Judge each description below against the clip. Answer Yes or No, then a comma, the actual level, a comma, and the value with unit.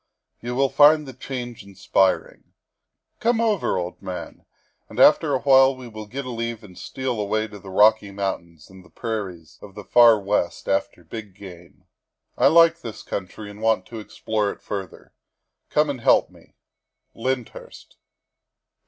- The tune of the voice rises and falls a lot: No, average, 4.6 semitones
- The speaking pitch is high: No, low, 110 Hz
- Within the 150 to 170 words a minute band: Yes, average, 165 wpm